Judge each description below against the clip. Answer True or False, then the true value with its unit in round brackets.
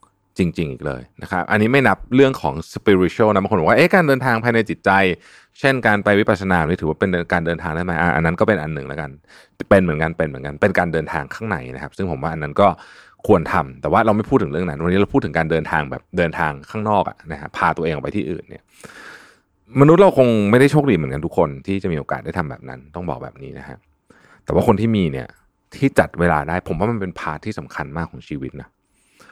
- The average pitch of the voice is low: True (95 Hz)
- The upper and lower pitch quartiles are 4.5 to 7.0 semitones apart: True (5.1 semitones)